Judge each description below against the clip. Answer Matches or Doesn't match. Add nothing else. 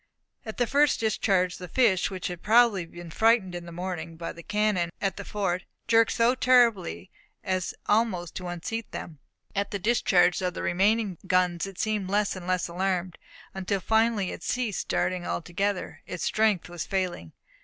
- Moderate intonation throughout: Matches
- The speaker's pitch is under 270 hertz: Matches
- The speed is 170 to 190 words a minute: Matches